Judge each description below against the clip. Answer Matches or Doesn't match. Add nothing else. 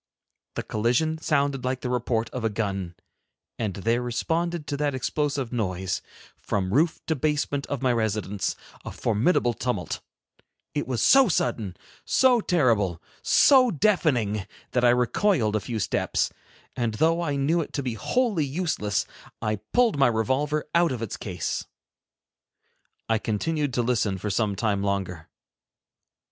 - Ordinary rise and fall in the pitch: Doesn't match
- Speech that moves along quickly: Doesn't match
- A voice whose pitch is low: Matches